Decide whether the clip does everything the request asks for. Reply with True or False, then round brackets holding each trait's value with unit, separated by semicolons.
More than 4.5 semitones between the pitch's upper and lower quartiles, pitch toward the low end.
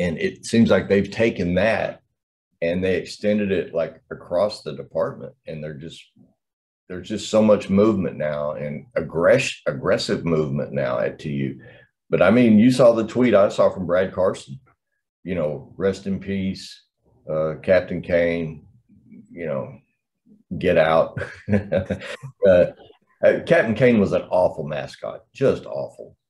True (5.2 semitones; 95 Hz)